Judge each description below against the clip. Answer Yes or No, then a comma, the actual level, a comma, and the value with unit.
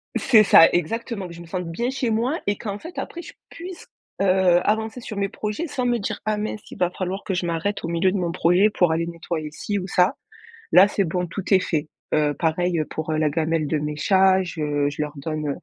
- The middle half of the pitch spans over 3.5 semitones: Yes, average, 4.4 semitones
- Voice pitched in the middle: Yes, medium, 180 Hz